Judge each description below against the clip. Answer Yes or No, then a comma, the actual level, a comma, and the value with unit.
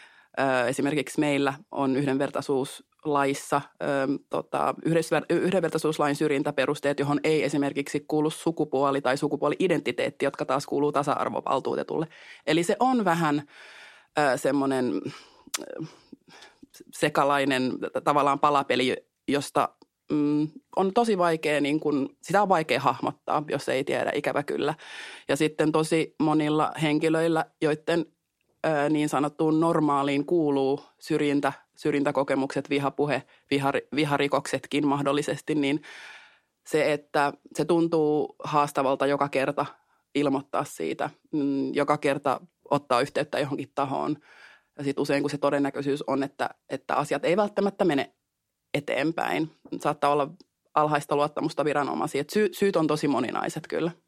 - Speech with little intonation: Yes, narrow, 2.0 semitones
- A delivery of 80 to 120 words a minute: Yes, average, 105 wpm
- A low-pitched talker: No, medium, 145 Hz